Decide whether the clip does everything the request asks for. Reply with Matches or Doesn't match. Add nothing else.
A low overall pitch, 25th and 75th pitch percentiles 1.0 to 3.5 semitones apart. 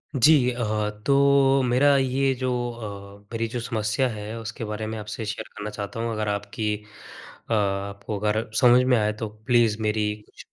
Matches